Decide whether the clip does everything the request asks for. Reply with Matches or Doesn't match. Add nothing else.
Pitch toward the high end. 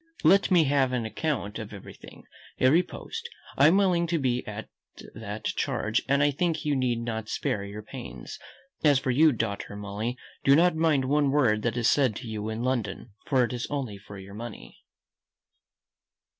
Doesn't match